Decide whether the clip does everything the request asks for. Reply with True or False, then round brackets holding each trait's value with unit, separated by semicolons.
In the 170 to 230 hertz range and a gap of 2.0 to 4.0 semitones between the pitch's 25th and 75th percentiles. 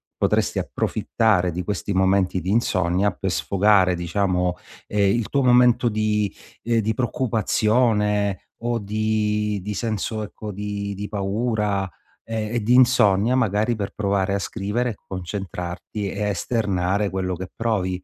False (105 Hz; 2.5 semitones)